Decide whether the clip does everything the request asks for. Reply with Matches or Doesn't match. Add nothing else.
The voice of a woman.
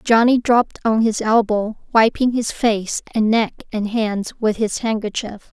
Matches